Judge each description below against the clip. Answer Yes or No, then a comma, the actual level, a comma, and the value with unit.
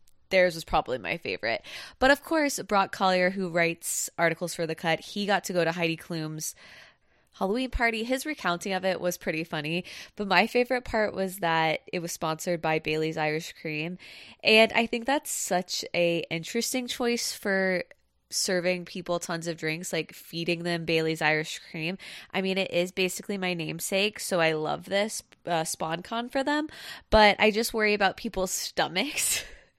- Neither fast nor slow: Yes, average, 175 wpm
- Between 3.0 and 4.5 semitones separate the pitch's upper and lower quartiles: Yes, average, 4.2 semitones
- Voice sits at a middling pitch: Yes, medium, 180 Hz